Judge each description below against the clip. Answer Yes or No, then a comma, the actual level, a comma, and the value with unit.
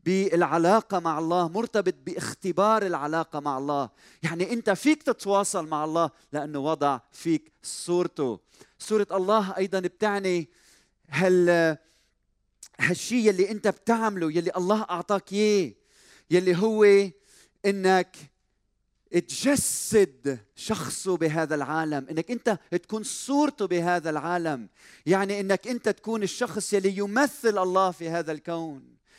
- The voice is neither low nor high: Yes, medium, 180 Hz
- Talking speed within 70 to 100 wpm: No, average, 115 wpm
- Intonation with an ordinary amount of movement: Yes, average, 4.1 semitones